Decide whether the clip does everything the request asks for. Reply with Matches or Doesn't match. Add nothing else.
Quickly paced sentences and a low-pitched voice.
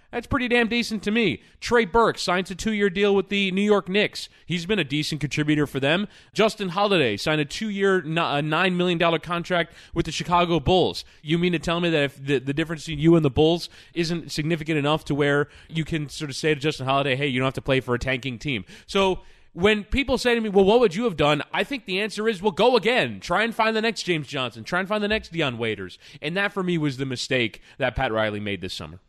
Doesn't match